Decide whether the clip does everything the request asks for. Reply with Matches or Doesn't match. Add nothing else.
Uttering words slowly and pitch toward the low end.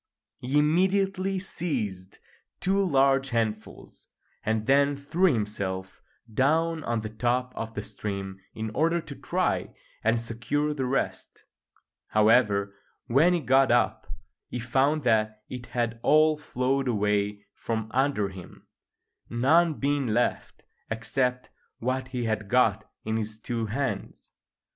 Matches